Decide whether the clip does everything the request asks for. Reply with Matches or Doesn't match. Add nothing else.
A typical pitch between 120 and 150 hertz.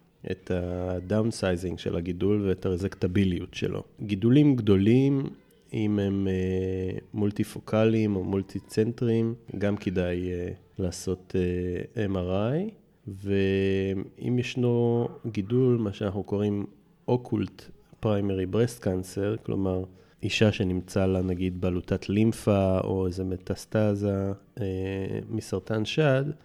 Doesn't match